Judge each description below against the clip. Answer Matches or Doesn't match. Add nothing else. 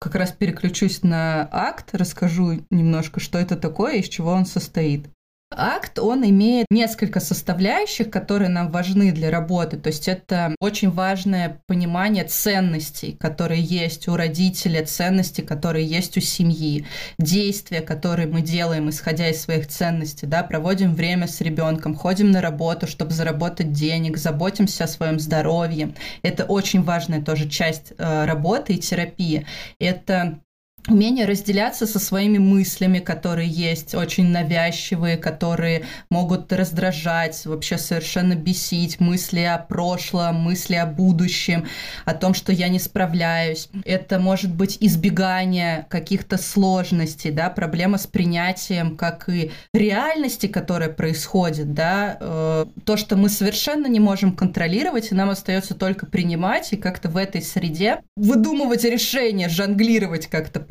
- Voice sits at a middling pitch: Matches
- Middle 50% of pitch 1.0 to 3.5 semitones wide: Matches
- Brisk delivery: Doesn't match